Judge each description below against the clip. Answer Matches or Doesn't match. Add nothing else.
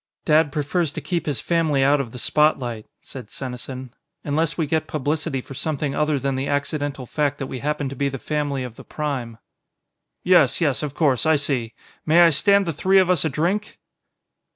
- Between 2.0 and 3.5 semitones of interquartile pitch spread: Matches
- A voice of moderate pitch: Matches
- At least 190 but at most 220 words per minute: Matches